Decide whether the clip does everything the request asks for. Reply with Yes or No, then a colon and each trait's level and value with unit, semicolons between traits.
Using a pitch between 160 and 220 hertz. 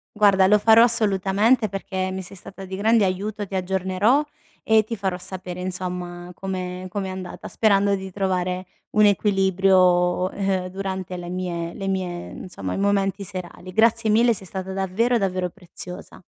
Yes: high, 190 Hz